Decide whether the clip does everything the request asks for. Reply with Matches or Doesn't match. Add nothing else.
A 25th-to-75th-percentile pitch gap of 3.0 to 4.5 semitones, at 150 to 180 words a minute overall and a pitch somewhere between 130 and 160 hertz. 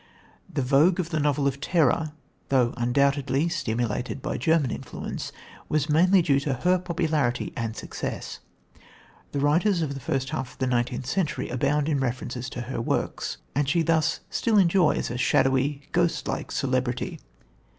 Matches